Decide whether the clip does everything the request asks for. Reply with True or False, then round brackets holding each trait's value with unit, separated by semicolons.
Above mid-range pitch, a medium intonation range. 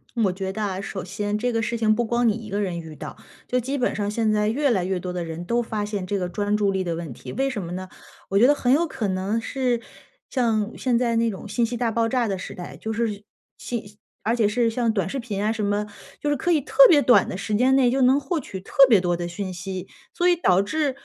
True (215 Hz; 4.1 semitones)